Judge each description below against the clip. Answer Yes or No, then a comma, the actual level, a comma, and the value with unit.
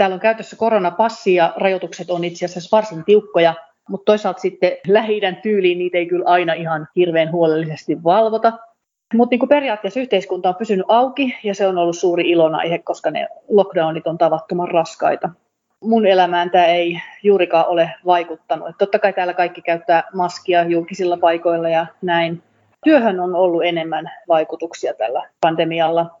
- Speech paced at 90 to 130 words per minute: No, fast, 155 wpm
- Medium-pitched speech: Yes, medium, 180 Hz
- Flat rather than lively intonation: No, average, 3.3 semitones